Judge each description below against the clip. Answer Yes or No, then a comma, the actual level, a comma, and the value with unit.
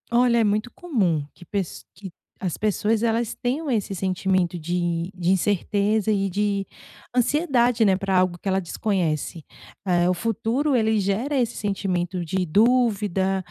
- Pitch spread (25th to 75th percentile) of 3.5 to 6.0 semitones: Yes, average, 3.8 semitones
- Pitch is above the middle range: Yes, high, 200 Hz